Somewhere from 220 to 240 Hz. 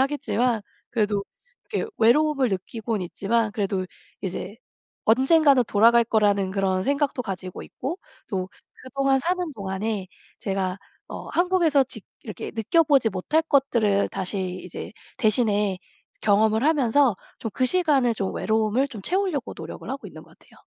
Yes: high, 225 Hz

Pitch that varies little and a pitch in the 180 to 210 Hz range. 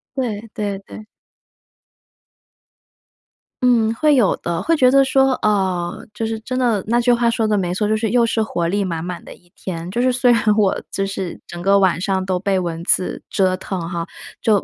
No: average, 4.2 semitones; high, 205 Hz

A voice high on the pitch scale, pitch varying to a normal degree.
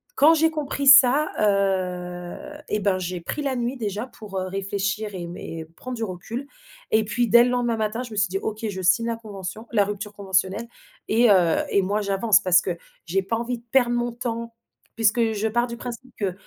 Yes: high, 215 Hz; average, 3.6 semitones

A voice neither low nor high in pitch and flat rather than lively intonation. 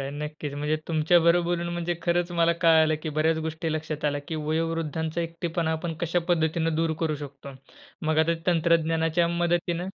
Yes: medium, 165 Hz; narrow, 1.5 semitones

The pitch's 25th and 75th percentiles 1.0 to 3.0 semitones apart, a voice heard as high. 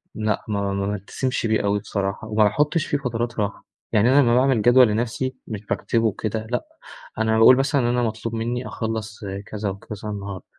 No: average, 2.7 semitones; low, 110 Hz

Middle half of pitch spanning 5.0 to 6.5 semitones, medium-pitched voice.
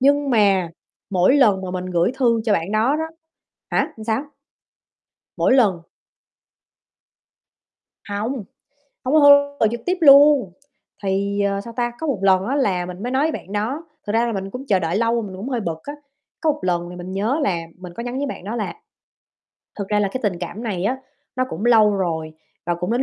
No: wide, 5.5 semitones; high, 215 Hz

